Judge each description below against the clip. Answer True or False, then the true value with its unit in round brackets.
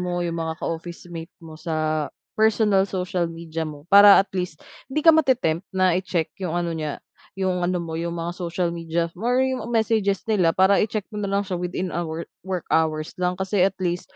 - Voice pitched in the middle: True (180 Hz)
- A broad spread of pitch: False (2.9 semitones)